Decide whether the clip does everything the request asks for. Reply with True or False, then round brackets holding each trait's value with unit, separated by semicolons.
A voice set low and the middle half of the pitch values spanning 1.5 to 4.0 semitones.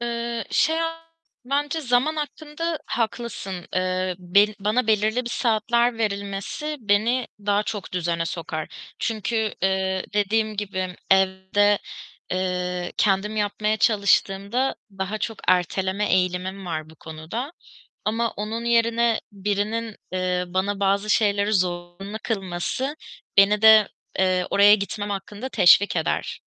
False (205 Hz; 3.3 semitones)